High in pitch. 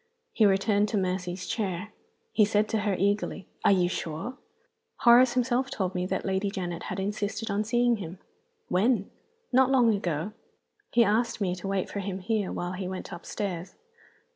Yes: high, 200 Hz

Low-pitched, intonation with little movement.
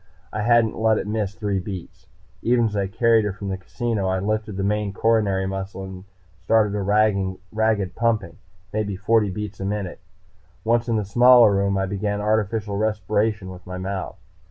Yes: low, 105 Hz; narrow, 2.2 semitones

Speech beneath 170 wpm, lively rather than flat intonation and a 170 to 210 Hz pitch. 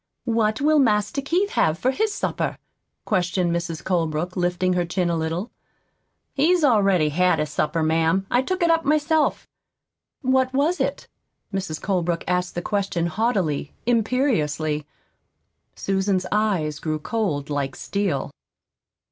Yes: slow, 135 wpm; wide, 6.9 semitones; high, 190 Hz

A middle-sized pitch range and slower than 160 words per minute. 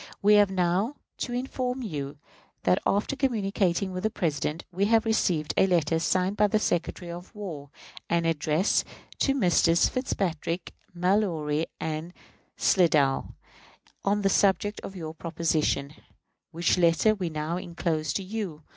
Yes: average, 4.2 semitones; average, 140 wpm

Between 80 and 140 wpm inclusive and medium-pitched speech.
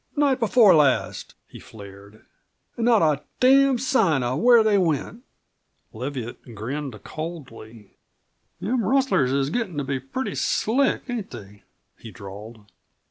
Yes: slow, 135 wpm; medium, 150 Hz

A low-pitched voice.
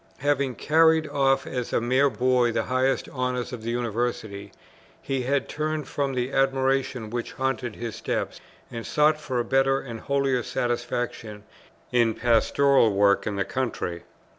Yes: low, 125 Hz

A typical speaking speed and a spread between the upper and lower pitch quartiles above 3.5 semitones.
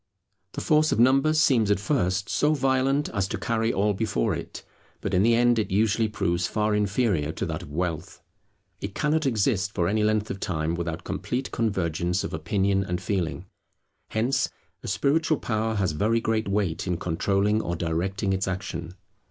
Yes: average, 175 wpm; average, 4.2 semitones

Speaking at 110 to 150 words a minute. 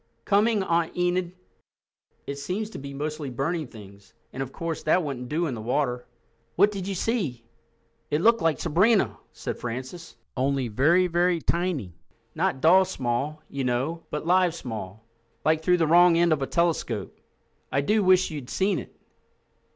No: average, 160 wpm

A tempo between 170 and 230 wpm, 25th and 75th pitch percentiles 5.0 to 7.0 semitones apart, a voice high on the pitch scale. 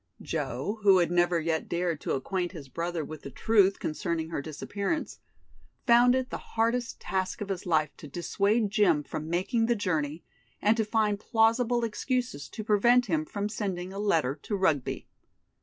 Yes: average, 175 wpm; average, 5.3 semitones; high, 195 Hz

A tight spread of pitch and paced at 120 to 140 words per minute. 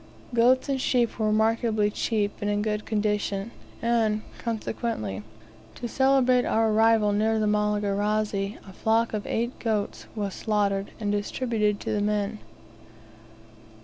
Yes: narrow, 1.7 semitones; slow, 135 wpm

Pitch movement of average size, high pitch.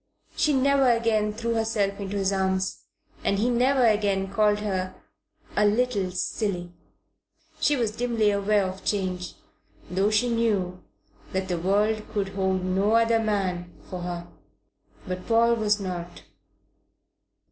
Yes: average, 3.2 semitones; high, 205 Hz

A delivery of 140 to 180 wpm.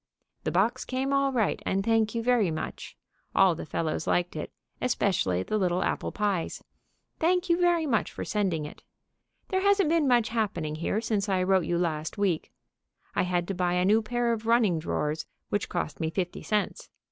No: average, 190 wpm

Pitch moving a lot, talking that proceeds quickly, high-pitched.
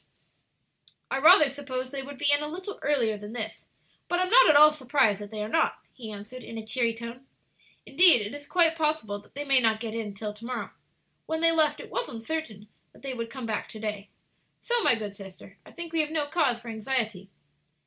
Yes: wide, 5.7 semitones; fast, 225 wpm; very high, 255 Hz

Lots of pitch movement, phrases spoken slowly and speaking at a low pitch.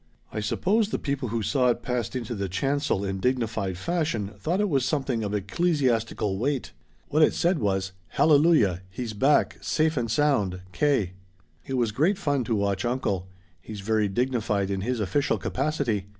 No: wide, 6.2 semitones; average, 175 wpm; low, 120 Hz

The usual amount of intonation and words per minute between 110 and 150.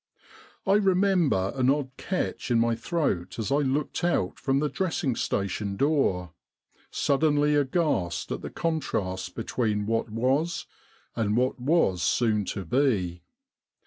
No: wide, 6.6 semitones; slow, 135 wpm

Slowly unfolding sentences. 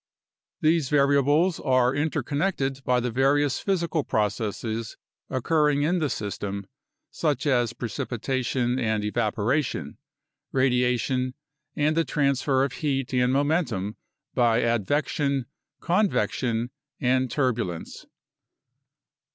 Yes: slow, 100 wpm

